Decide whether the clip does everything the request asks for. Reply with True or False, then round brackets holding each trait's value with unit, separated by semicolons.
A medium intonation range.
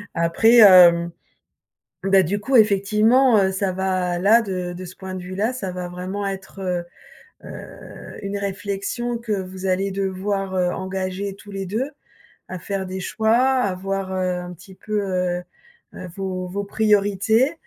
False (1.9 semitones)